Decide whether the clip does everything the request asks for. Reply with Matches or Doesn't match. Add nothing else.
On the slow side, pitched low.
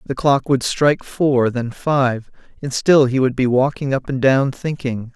Doesn't match